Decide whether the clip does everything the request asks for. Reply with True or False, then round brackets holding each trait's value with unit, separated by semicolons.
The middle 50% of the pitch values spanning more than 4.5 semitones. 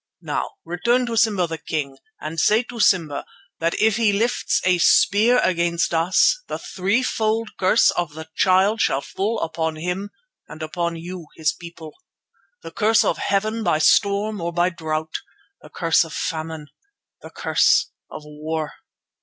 True (4.9 semitones)